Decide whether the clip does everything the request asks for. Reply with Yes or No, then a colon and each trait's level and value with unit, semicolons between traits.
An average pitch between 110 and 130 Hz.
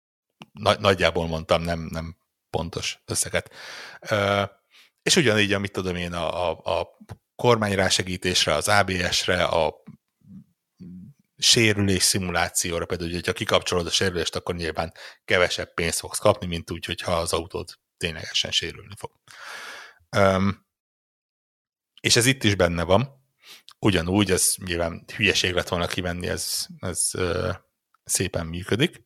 No: very low, 95 Hz